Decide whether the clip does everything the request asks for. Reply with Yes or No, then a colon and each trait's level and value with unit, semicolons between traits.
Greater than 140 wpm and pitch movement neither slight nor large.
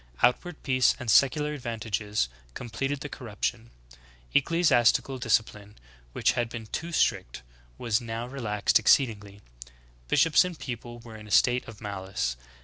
No: slow, 135 wpm; average, 4.1 semitones